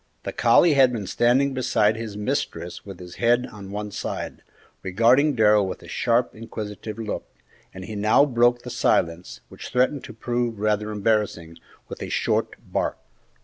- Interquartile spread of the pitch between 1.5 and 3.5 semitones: Yes, average, 2.9 semitones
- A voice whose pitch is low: Yes, low, 110 Hz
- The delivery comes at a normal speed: Yes, average, 165 wpm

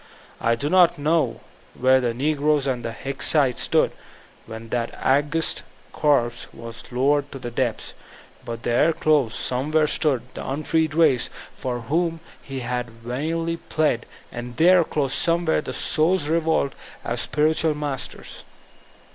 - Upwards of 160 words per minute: No, average, 140 wpm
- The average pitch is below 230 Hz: Yes, medium, 140 Hz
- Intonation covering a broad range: No, average, 4.3 semitones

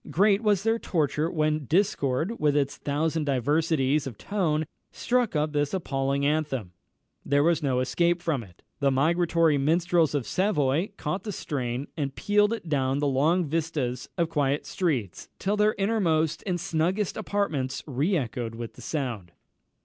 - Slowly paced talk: No, average, 155 wpm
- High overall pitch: No, medium, 155 Hz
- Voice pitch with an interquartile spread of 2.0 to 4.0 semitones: No, average, 4.4 semitones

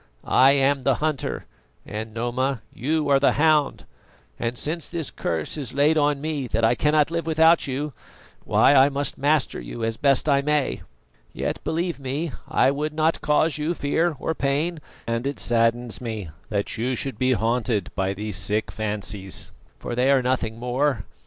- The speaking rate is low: No, average, 170 wpm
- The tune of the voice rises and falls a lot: No, average, 4.5 semitones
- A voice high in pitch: No, low, 135 Hz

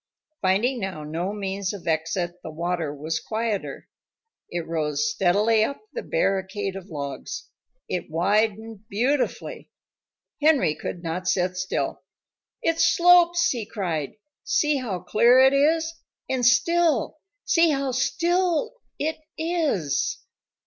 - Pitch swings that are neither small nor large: No, wide, 8.1 semitones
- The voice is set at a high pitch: Yes, high, 210 Hz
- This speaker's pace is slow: Yes, slow, 120 wpm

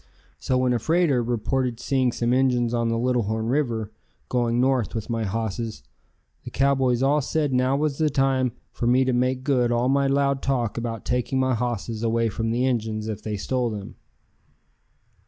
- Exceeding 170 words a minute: Yes, average, 185 wpm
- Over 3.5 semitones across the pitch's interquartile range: No, narrow, 2.5 semitones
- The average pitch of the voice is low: Yes, low, 125 Hz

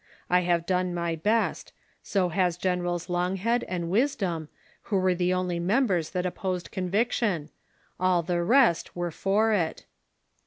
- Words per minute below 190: Yes, average, 145 wpm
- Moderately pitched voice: Yes, medium, 180 Hz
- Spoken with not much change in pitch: Yes, narrow, 2.0 semitones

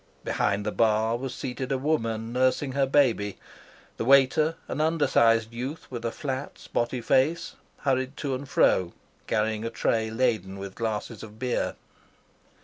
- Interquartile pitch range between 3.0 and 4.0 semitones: Yes, average, 3.3 semitones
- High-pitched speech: No, low, 120 Hz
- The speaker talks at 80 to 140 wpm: No, average, 150 wpm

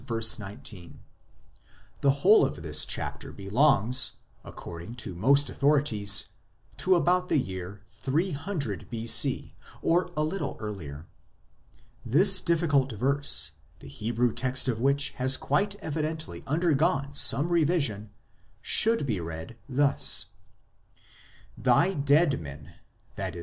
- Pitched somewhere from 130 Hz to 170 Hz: Yes, low, 135 Hz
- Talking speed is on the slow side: Yes, slow, 115 wpm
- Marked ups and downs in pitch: Yes, wide, 6.7 semitones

